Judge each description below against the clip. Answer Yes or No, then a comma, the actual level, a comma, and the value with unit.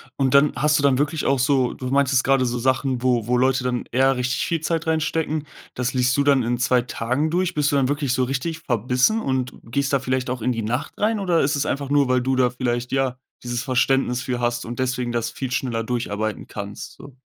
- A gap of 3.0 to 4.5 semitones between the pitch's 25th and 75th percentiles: No, narrow, 2.4 semitones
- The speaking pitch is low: Yes, low, 130 Hz